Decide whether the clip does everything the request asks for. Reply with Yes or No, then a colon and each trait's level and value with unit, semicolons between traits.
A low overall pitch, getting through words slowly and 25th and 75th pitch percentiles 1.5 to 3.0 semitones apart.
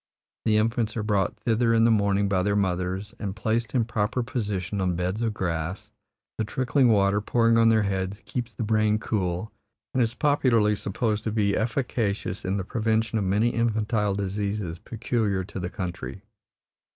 No: low, 105 Hz; average, 175 wpm; narrow, 2.6 semitones